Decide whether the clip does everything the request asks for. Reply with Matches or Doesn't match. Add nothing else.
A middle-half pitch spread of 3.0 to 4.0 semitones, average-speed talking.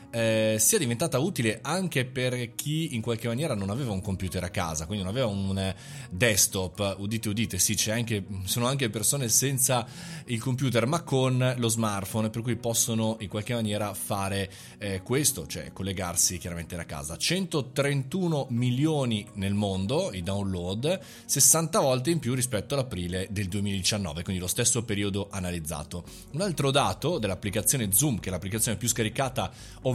Doesn't match